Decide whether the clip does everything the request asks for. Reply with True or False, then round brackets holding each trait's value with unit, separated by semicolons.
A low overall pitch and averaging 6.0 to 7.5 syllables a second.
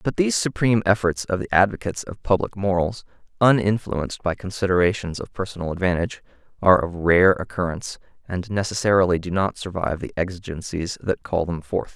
True (95 Hz; 6.1 syllables/s)